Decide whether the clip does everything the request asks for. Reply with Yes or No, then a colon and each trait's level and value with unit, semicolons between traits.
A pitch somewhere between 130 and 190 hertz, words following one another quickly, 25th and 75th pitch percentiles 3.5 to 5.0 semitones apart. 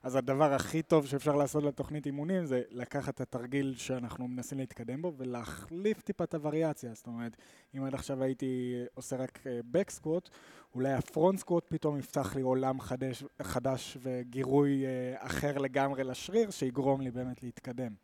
No: low, 135 Hz; fast, 155 wpm; narrow, 2.6 semitones